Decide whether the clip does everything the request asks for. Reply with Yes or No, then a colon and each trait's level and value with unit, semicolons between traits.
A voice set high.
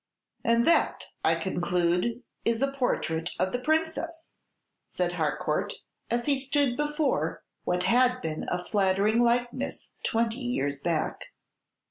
Yes: high, 235 Hz